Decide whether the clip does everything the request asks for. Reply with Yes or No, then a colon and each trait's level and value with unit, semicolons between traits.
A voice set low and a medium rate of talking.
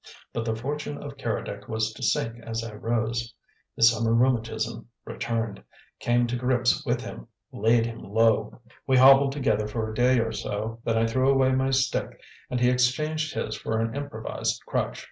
Yes: low, 115 Hz; average, 180 wpm